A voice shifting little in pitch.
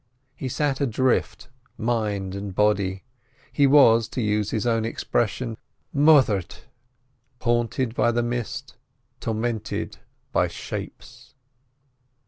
No: average, 3.0 semitones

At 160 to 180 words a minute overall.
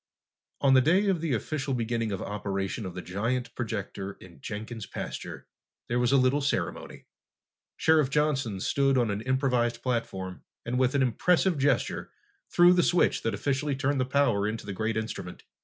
Yes: average, 175 wpm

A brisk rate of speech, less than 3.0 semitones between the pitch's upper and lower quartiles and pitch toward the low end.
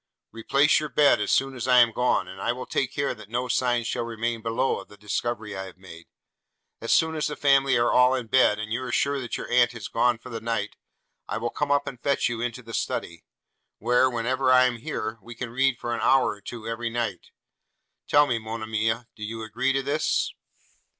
Yes: fast, 225 wpm; narrow, 2.5 semitones; low, 120 Hz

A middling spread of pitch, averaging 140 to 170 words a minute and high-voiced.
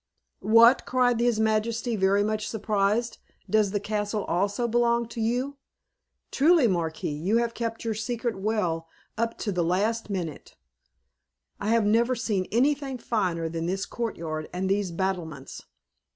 Yes: average, 3.6 semitones; average, 145 wpm; high, 215 Hz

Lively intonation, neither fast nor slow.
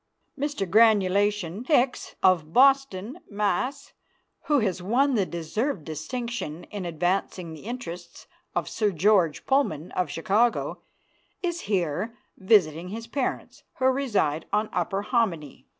No: wide, 5.7 semitones; slow, 120 wpm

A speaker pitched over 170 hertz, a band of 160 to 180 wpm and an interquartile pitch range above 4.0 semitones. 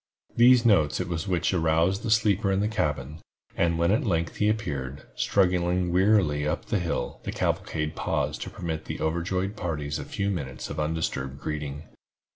No: very low, 85 Hz; average, 175 wpm; average, 4.5 semitones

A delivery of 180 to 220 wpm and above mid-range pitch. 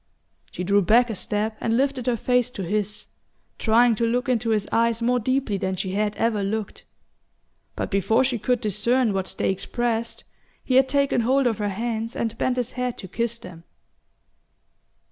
Yes: average, 185 wpm; high, 230 Hz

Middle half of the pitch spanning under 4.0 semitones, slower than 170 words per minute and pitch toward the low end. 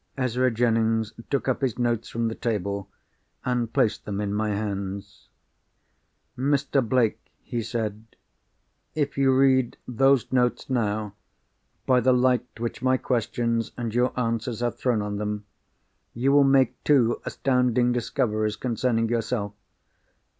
Yes: average, 2.8 semitones; slow, 135 wpm; low, 120 Hz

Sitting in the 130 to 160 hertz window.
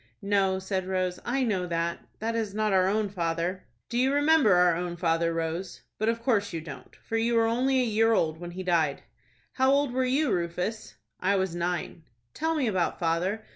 No: high, 190 Hz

